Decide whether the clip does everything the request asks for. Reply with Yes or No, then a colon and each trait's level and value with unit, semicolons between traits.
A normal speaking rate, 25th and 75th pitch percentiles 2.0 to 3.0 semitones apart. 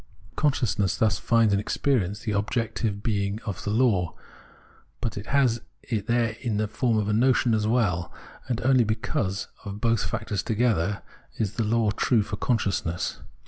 Yes: average, 160 wpm; narrow, 2.5 semitones